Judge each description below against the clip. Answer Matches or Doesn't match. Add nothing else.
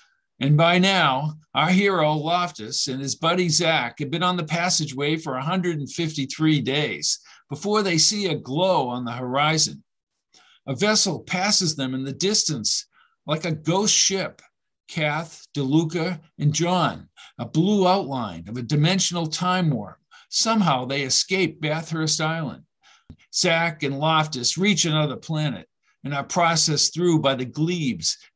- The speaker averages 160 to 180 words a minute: Doesn't match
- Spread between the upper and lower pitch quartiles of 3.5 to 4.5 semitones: Matches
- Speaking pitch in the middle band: Matches